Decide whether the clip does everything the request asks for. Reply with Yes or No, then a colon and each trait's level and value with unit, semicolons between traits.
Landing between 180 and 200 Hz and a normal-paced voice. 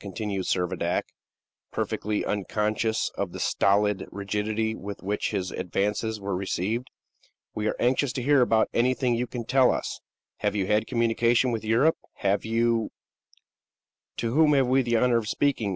No: low, 110 Hz; average, 155 wpm